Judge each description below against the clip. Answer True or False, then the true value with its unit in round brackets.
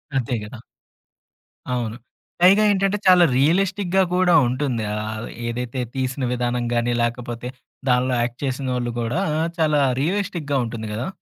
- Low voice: True (130 Hz)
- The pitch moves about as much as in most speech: False (6.4 semitones)